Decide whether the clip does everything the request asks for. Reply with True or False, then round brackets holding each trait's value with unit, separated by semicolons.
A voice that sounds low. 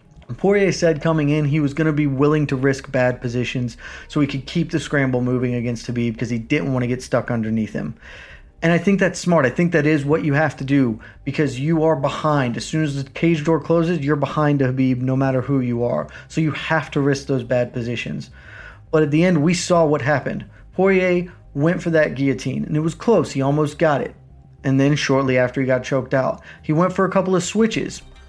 False (145 Hz)